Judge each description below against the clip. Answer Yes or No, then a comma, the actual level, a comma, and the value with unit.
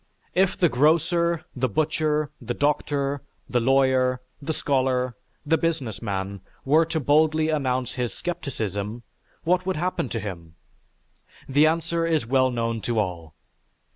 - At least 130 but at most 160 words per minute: Yes, average, 140 wpm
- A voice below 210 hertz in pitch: Yes, low, 135 Hz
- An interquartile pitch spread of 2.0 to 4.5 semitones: No, average, 5.0 semitones